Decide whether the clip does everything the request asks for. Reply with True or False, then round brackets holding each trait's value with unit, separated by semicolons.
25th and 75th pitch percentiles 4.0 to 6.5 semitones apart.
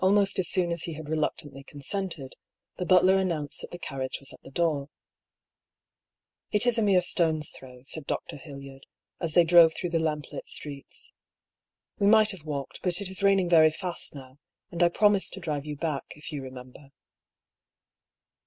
True (4.4 semitones)